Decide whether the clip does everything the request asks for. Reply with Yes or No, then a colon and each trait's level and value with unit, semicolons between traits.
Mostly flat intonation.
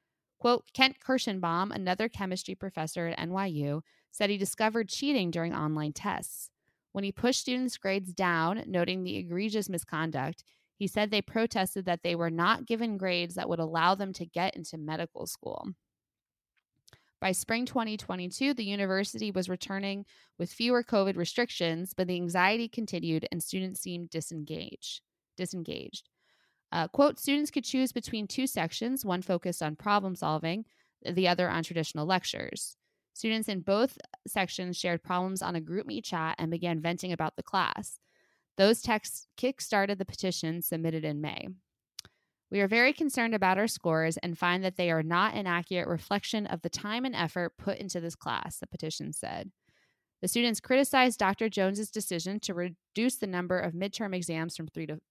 No: average, 4.1 semitones